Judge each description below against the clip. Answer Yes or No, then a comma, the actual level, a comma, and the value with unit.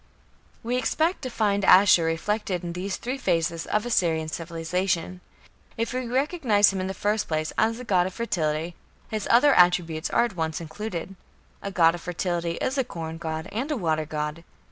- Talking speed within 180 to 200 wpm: Yes, average, 190 wpm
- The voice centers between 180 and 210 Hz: Yes, medium, 185 Hz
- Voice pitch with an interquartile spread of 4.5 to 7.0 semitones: Yes, wide, 5.4 semitones